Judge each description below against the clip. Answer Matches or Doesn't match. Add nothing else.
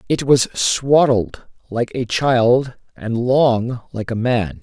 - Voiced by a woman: Doesn't match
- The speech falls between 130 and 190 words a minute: Matches